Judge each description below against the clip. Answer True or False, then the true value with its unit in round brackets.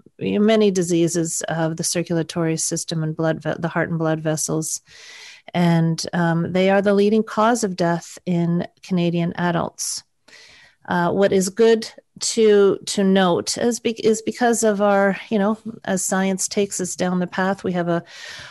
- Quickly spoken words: False (165 wpm)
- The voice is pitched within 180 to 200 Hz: True (185 Hz)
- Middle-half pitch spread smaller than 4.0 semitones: True (3.6 semitones)